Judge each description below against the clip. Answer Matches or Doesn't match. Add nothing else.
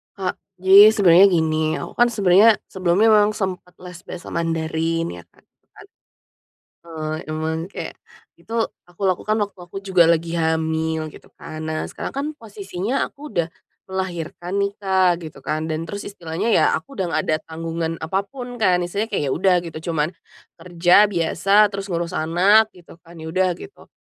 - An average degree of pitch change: Matches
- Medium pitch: Matches